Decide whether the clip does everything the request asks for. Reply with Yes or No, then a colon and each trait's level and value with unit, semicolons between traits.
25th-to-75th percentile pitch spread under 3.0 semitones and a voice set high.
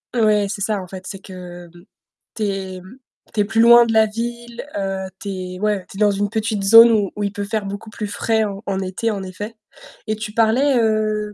Yes: narrow, 2.4 semitones; high, 210 Hz